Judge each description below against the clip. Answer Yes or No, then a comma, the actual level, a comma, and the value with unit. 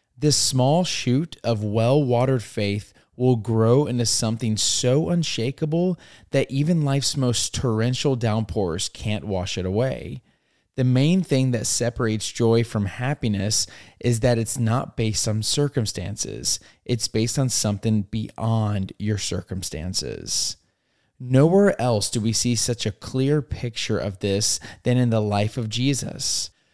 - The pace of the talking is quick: No, average, 140 wpm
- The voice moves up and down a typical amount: Yes, average, 3.5 semitones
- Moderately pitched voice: No, low, 115 Hz